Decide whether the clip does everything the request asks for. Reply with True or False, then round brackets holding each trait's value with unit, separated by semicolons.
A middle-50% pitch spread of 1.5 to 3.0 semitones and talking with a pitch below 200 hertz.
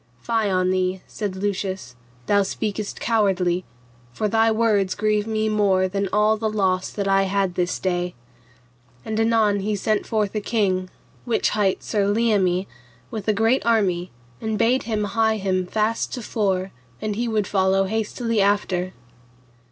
False (2.6 semitones; 205 Hz)